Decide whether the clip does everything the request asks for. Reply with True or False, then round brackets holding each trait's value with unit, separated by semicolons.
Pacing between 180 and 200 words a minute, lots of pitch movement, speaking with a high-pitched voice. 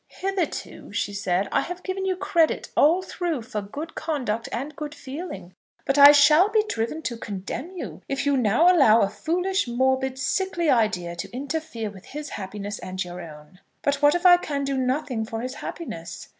True (185 wpm; 7.3 semitones; 275 Hz)